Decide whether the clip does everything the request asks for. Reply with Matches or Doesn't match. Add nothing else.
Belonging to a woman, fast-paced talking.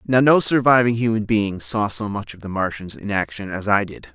Doesn't match